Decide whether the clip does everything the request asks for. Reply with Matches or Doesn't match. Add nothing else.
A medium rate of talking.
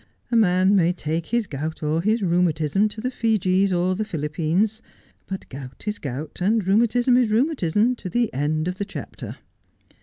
Matches